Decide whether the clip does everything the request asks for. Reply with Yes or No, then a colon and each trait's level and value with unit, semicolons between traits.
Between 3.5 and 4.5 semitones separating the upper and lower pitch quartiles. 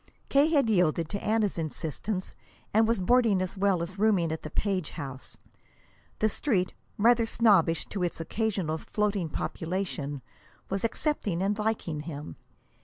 No: average, 4.9 semitones